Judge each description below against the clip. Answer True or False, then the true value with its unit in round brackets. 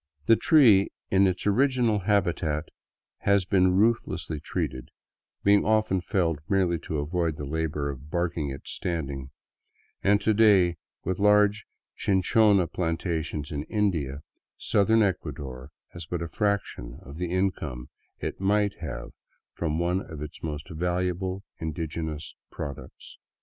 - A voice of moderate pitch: False (90 Hz)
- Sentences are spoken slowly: True (130 wpm)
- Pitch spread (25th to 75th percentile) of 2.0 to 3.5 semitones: False (4.5 semitones)